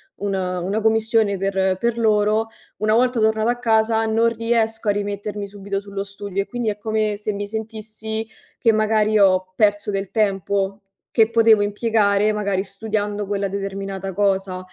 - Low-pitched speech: No, high, 210 Hz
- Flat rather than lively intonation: Yes, narrow, 1.8 semitones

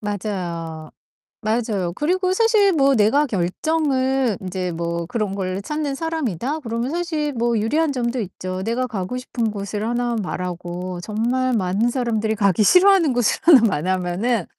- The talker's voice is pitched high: Yes, high, 225 Hz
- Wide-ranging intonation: Yes, wide, 6.4 semitones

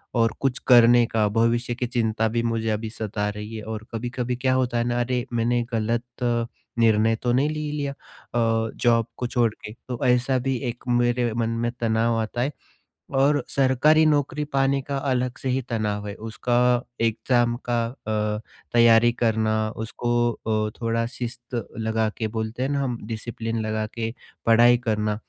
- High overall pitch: No, low, 120 Hz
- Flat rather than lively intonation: Yes, narrow, 1.8 semitones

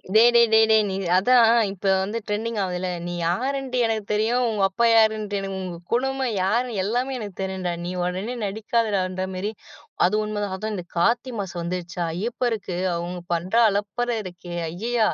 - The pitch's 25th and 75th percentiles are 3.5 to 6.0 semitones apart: Yes, average, 3.8 semitones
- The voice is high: Yes, high, 210 Hz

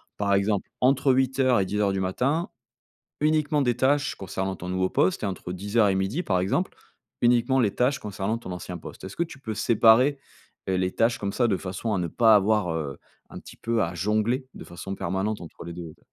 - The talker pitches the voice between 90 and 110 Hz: Yes, low, 105 Hz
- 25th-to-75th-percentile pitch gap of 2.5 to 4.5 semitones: No, average, 4.9 semitones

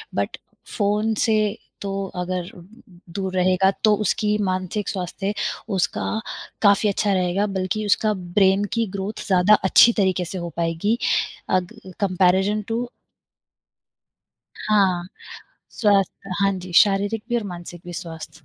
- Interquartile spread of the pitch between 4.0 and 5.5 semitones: No, narrow, 2.5 semitones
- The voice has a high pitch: Yes, high, 195 Hz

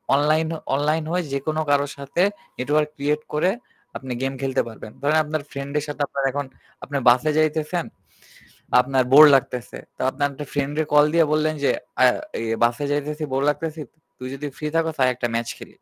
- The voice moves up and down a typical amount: No, narrow, 2.2 semitones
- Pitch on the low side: No, medium, 145 Hz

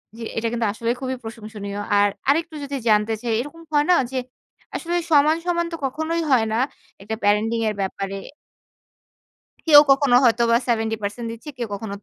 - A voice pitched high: Yes, high, 235 Hz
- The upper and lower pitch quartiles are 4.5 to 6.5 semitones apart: Yes, average, 5.0 semitones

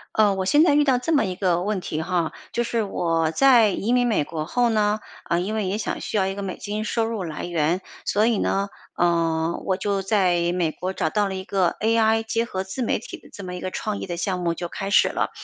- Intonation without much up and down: No, average, 3.8 semitones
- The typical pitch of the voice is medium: No, high, 195 Hz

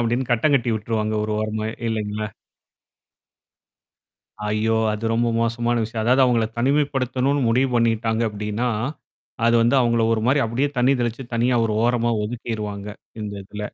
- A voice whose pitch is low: Yes, low, 115 Hz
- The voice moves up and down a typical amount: No, narrow, 2.2 semitones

